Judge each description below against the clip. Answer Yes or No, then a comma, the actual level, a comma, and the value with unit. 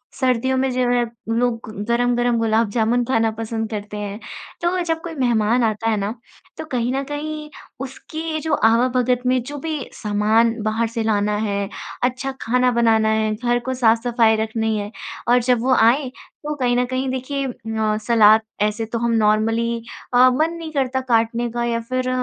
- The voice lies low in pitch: No, high, 235 Hz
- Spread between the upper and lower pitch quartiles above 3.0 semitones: No, narrow, 2.6 semitones